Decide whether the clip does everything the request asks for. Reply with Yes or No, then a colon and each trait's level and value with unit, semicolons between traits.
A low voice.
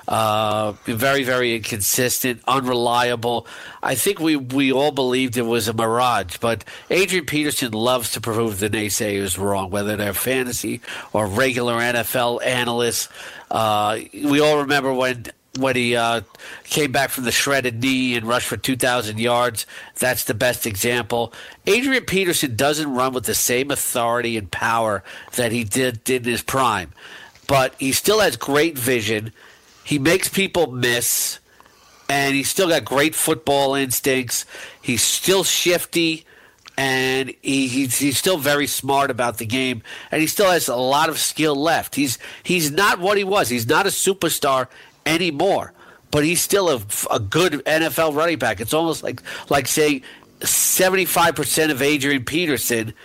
Yes: low, 130 Hz